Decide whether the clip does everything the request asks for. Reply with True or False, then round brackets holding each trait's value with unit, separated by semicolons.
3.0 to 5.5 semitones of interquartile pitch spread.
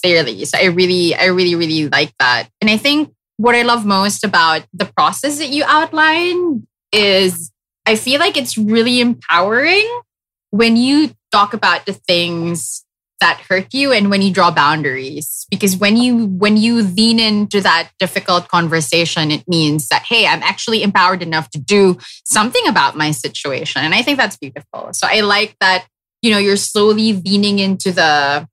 True (4.9 semitones)